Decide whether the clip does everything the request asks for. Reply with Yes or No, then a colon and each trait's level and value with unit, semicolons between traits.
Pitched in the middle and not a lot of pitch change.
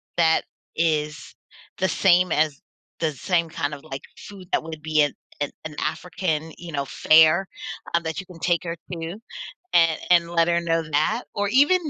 Yes: medium, 165 Hz; narrow, 2.2 semitones